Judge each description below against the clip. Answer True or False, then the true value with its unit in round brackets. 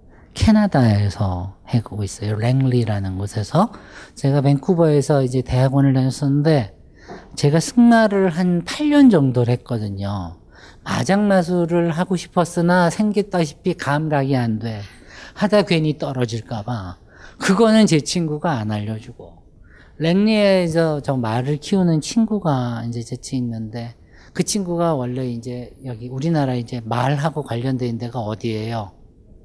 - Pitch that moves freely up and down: True (6.8 semitones)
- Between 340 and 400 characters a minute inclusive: False (290 characters per minute)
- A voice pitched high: False (135 Hz)